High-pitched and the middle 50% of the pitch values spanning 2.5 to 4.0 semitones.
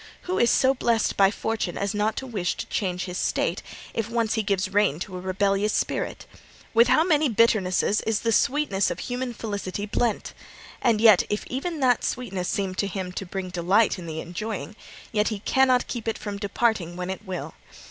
Yes: high, 210 Hz; average, 3.6 semitones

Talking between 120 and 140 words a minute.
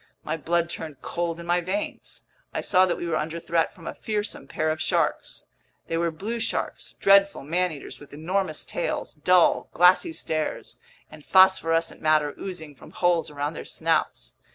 No: average, 175 wpm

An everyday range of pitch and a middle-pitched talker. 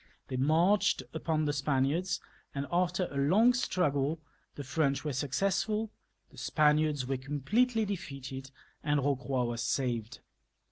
Yes: average, 4.8 semitones; medium, 145 Hz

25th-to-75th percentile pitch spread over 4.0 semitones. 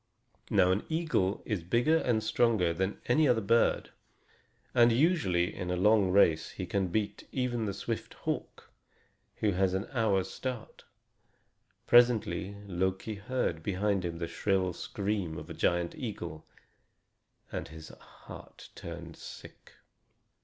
Yes: average, 4.5 semitones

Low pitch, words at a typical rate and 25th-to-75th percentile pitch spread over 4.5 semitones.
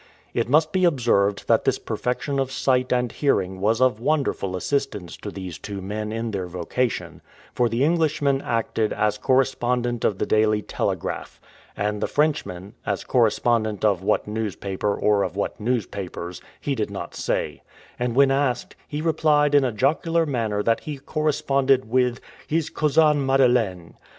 Yes: low, 120 Hz; average, 160 wpm; average, 4.9 semitones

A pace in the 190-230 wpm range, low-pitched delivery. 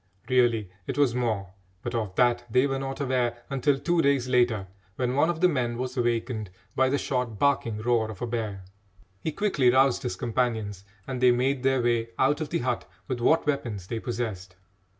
Yes: average, 195 wpm; low, 125 Hz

